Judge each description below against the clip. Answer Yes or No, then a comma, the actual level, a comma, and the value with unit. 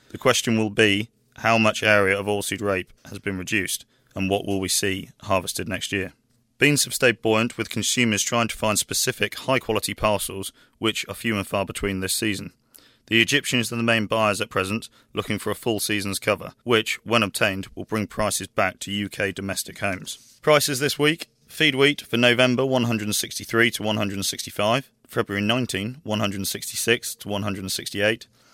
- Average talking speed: Yes, average, 170 wpm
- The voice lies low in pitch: Yes, low, 110 Hz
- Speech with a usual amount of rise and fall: Yes, average, 3.0 semitones